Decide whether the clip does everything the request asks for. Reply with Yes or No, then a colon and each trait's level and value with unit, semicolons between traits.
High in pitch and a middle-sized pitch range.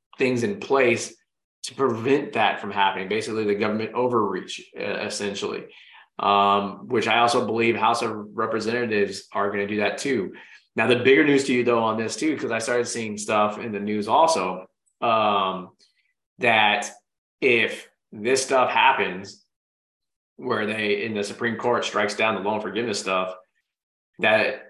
No: low, 110 Hz; average, 3.1 semitones